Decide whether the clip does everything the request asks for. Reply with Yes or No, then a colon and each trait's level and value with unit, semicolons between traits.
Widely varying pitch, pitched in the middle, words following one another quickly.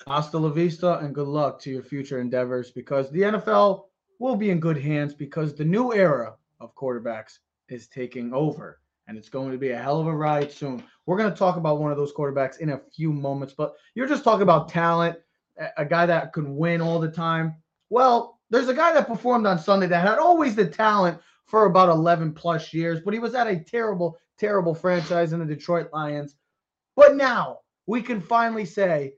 Yes: wide, 5.7 semitones; medium, 165 Hz; fast, 210 wpm